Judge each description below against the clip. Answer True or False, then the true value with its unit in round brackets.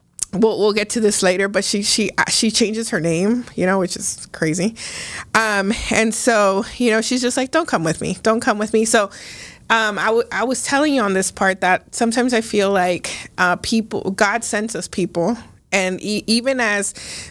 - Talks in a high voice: True (210 Hz)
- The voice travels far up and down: False (3.2 semitones)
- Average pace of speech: False (210 wpm)